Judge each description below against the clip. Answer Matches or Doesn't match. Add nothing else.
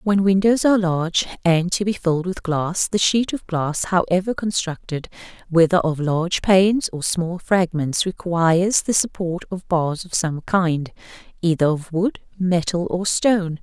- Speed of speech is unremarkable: Matches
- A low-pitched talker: Doesn't match